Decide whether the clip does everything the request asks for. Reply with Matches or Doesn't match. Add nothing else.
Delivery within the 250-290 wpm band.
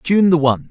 Matches